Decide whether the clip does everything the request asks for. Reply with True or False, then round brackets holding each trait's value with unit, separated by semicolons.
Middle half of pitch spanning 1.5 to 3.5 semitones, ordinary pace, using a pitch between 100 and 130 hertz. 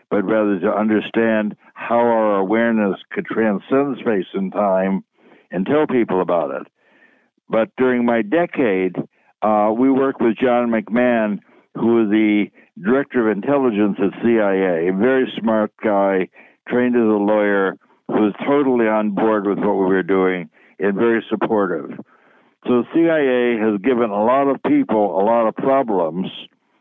True (3.0 semitones; 155 wpm; 110 Hz)